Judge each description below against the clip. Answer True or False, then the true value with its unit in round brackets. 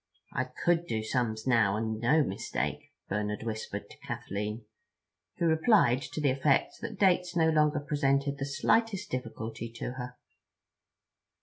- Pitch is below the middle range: True (130 Hz)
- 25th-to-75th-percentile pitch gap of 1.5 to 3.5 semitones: False (5.5 semitones)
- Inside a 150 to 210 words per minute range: False (140 wpm)